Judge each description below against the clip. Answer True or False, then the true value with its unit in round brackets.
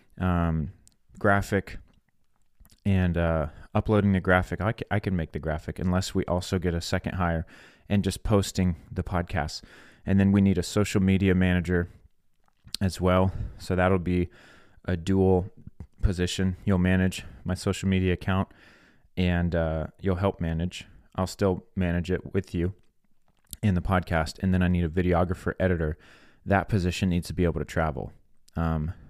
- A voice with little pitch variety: True (2.1 semitones)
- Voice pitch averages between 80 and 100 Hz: True (90 Hz)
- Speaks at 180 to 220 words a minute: False (155 wpm)